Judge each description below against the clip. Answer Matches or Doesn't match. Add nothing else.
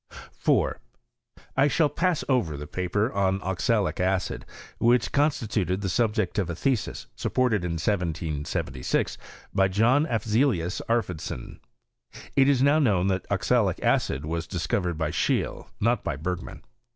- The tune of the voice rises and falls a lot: Matches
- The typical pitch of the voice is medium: Doesn't match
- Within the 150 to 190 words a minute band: Doesn't match